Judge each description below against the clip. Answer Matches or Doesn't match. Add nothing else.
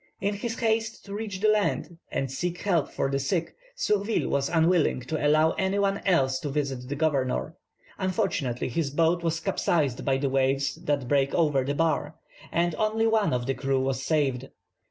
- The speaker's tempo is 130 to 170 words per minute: Doesn't match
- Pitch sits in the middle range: Matches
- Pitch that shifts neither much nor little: Doesn't match